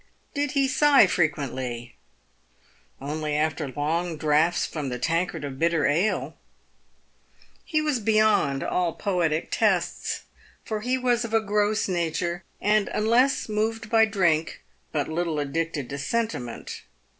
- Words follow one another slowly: Yes, slow, 130 wpm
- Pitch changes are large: Yes, wide, 6.3 semitones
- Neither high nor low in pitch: Yes, medium, 175 Hz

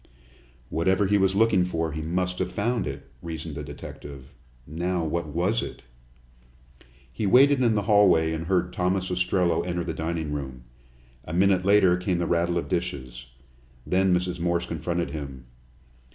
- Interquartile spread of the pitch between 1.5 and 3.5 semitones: Yes, average, 2.8 semitones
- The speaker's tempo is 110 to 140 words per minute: No, average, 160 wpm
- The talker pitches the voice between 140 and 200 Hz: No, very low, 90 Hz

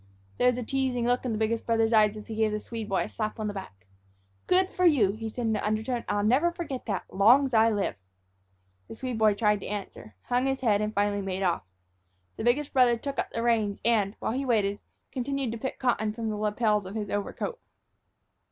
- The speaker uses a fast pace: Yes, fast, 230 wpm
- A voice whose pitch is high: Yes, high, 225 Hz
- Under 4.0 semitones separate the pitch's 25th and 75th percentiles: Yes, average, 3.0 semitones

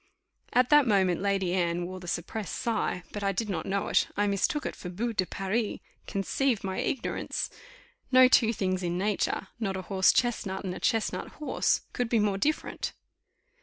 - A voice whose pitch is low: No, high, 200 Hz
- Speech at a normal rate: Yes, average, 185 wpm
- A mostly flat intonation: No, average, 3.6 semitones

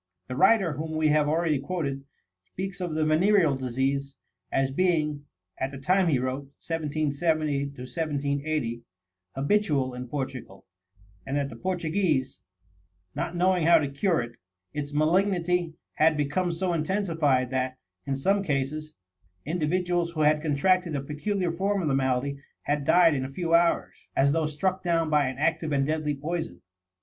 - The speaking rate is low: No, average, 155 wpm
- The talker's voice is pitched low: No, medium, 155 Hz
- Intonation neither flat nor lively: Yes, average, 3.7 semitones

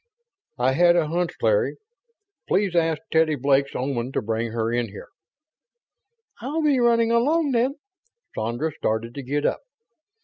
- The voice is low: No, medium, 155 Hz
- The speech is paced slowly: No, average, 145 wpm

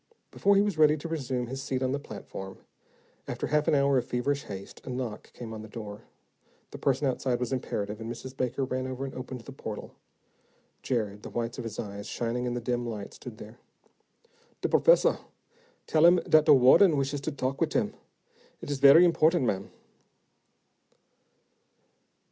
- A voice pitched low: Yes, low, 130 Hz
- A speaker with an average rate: Yes, average, 185 wpm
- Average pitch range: Yes, average, 3.6 semitones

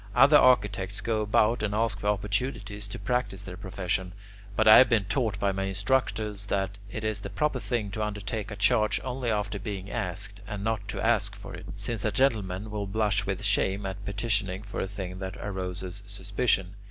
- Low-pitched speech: Yes, low, 105 Hz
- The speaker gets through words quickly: No, average, 195 wpm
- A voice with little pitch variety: Yes, narrow, 2.0 semitones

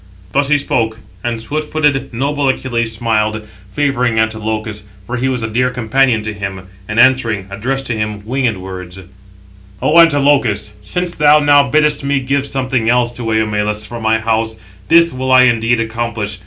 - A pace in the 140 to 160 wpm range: No, average, 170 wpm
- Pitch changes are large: No, average, 3.7 semitones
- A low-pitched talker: Yes, low, 120 Hz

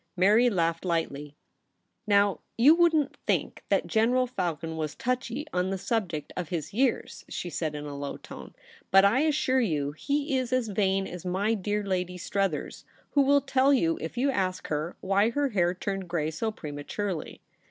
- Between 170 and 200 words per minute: Yes, average, 195 wpm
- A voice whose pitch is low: No, high, 195 Hz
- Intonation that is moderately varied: No, wide, 6.8 semitones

